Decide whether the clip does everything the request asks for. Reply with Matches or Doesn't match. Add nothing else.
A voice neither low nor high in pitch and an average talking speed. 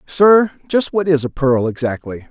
Matches